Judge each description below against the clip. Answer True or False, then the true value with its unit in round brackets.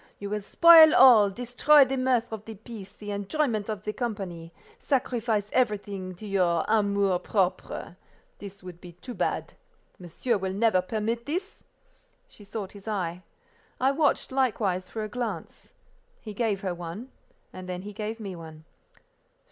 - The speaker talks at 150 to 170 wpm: True (155 wpm)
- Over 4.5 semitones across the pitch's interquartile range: False (4.1 semitones)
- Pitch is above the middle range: True (210 Hz)